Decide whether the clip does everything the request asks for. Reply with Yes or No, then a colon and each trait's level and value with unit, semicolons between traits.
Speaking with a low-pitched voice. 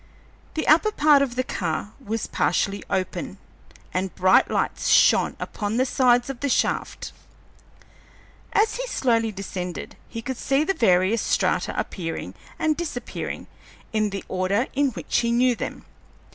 No: high, 235 Hz